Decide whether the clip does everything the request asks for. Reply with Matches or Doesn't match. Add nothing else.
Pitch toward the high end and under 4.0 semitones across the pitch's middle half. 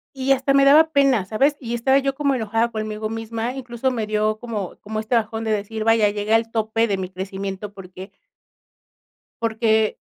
Matches